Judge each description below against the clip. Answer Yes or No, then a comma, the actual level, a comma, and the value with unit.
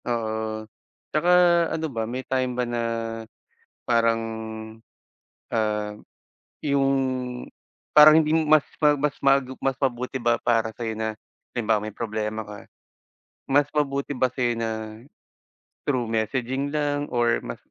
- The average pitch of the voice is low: Yes, low, 125 Hz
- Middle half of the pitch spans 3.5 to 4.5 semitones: Yes, average, 3.9 semitones